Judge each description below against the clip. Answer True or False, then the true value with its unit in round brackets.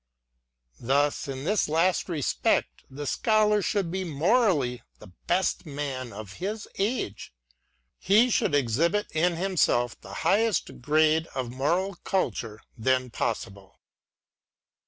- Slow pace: True (120 wpm)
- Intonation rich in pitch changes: True (6.9 semitones)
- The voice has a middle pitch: True (155 Hz)